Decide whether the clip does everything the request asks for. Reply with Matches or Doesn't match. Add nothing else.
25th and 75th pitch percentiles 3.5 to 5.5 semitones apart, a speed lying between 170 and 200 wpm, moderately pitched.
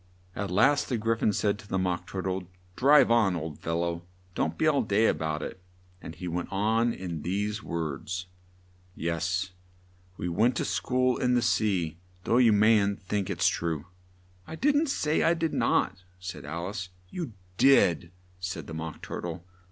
Doesn't match